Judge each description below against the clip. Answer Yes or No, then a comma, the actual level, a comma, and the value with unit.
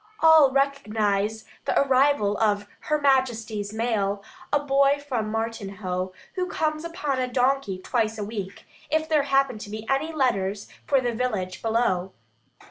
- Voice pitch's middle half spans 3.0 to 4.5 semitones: No, average, 5.0 semitones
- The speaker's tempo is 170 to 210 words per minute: No, average, 145 wpm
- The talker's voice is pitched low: No, high, 235 Hz